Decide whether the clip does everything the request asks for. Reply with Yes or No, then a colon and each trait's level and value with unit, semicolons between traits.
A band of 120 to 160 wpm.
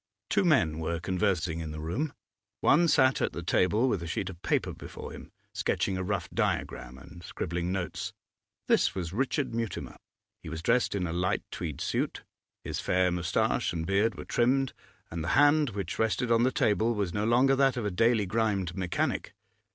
No: average, 190 wpm